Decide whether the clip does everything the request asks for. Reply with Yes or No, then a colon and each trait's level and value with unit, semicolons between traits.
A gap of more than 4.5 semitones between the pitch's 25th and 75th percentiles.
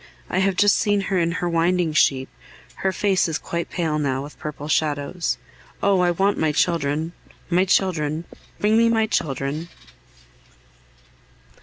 No: average, 3.9 semitones